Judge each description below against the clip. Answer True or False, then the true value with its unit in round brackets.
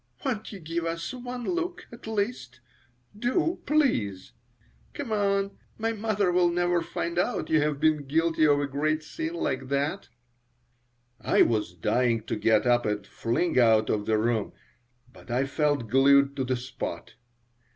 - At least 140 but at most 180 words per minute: True (155 wpm)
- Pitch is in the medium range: True (155 Hz)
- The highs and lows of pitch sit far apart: True (8.5 semitones)